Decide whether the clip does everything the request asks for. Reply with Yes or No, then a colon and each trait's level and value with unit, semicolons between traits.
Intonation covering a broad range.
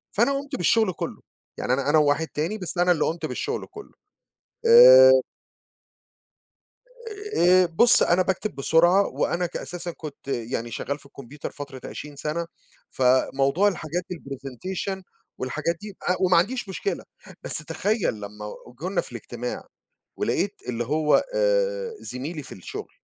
Yes: wide, 6.4 semitones